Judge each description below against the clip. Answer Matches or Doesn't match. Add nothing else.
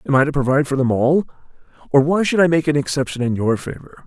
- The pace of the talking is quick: Matches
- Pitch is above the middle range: Doesn't match